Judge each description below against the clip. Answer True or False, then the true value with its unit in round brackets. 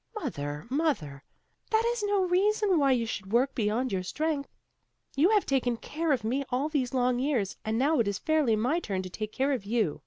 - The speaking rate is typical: False (210 wpm)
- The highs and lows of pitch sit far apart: True (6.4 semitones)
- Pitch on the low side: False (260 Hz)